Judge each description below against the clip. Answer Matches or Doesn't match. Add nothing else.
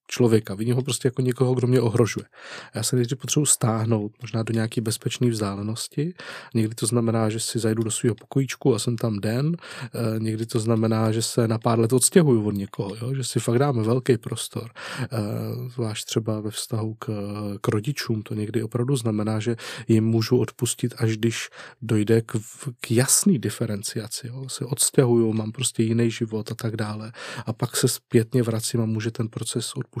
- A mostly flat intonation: Matches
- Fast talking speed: Matches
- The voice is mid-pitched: Doesn't match